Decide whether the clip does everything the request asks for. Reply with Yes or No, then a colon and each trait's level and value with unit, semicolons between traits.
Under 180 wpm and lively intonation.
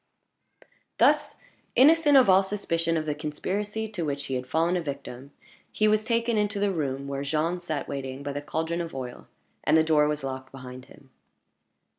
No: average, 185 wpm; wide, 6.1 semitones